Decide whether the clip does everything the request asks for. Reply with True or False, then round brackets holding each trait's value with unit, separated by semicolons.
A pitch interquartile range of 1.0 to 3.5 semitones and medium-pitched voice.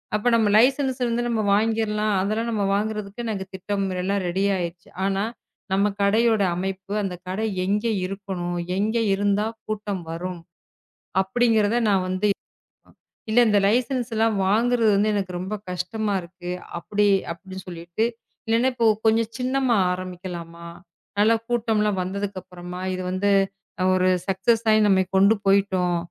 False (3.0 semitones; 200 Hz)